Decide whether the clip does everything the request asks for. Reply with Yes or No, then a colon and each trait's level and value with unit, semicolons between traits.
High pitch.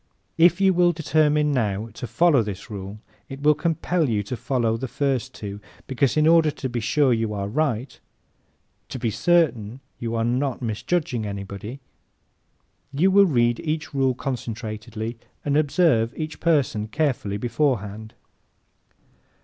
No: low, 125 Hz